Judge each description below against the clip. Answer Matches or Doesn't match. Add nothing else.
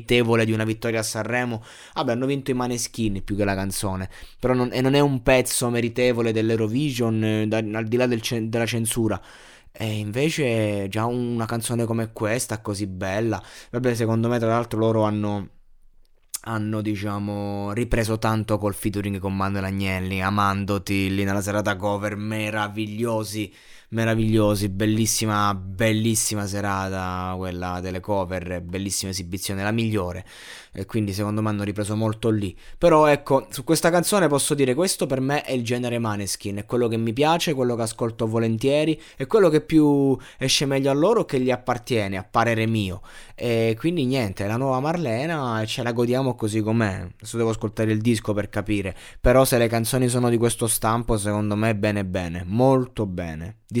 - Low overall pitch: Matches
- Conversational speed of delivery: Doesn't match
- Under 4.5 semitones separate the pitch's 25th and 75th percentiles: Matches